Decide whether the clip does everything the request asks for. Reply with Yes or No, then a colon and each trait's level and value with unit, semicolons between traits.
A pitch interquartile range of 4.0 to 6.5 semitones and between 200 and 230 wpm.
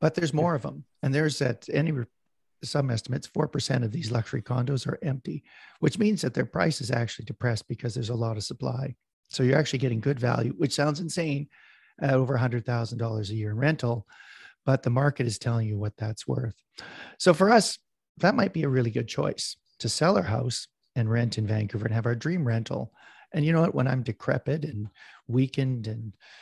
Yes: average, 4.4 semitones; fast, 205 wpm